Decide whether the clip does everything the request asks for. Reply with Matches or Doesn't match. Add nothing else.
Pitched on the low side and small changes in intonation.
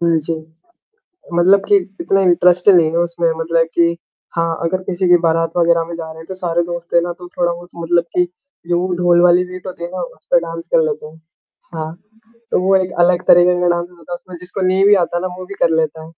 Doesn't match